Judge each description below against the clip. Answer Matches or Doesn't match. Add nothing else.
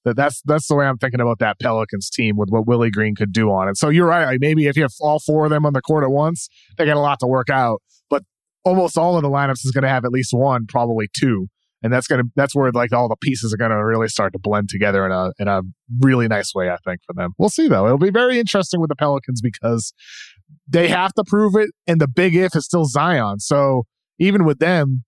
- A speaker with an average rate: Doesn't match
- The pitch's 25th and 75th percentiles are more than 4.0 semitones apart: Matches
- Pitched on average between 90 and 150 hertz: Matches